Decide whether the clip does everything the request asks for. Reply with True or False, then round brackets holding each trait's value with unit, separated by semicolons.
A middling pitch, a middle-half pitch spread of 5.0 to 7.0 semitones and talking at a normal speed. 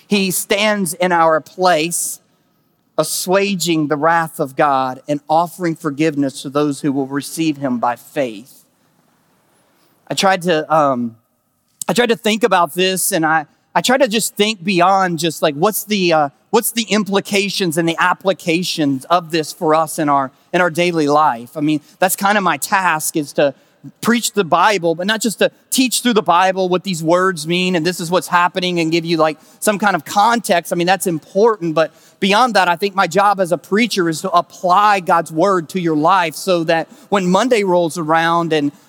False (175 Hz; 3.7 semitones; 195 wpm)